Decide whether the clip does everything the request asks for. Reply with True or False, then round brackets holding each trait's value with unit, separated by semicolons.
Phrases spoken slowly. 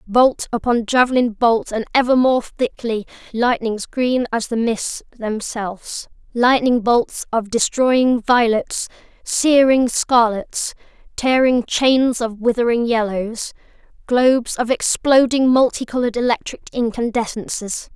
True (105 wpm)